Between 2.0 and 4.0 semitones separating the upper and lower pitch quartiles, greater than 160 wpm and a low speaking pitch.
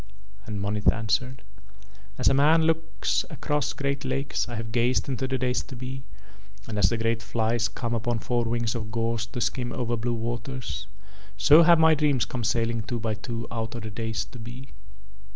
Yes: narrow, 2.6 semitones; average, 190 wpm; low, 120 Hz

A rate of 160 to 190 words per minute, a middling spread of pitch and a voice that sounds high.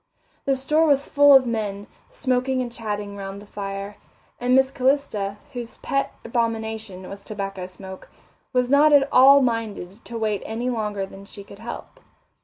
Yes: average, 165 wpm; average, 4.4 semitones; high, 225 Hz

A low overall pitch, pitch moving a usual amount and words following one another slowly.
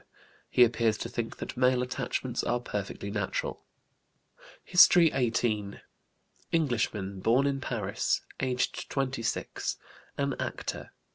Yes: low, 120 Hz; average, 3.6 semitones; slow, 110 wpm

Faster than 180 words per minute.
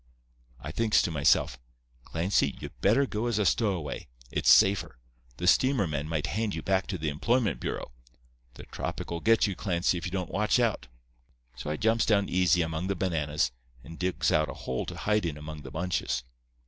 Yes: average, 190 wpm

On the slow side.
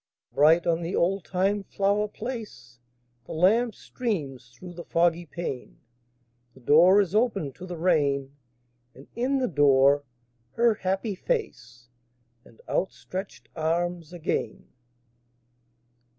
Yes: slow, 115 wpm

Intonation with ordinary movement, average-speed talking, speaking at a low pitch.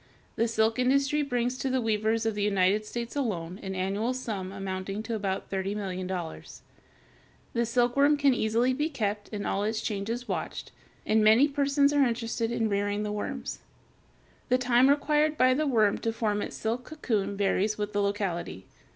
No: average, 3.9 semitones; average, 170 wpm; high, 220 Hz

